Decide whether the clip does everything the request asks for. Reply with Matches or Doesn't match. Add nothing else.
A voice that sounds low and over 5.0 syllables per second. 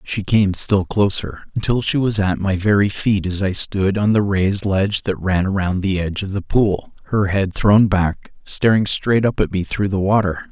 Doesn't match